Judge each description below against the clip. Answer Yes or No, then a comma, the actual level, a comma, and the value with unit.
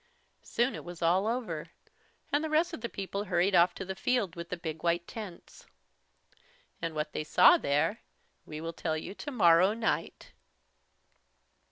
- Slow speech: No, average, 165 wpm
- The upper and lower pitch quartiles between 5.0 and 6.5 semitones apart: Yes, average, 5.3 semitones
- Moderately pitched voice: Yes, medium, 180 Hz